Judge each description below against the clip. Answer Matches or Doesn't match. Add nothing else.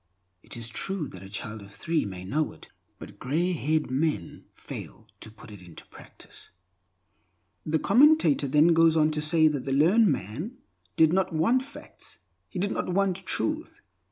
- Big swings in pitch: Matches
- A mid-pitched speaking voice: Matches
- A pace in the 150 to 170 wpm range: Doesn't match